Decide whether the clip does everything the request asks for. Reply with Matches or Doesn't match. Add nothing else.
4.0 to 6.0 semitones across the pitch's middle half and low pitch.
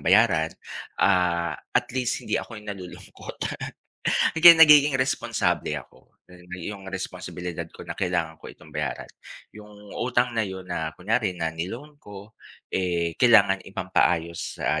Matches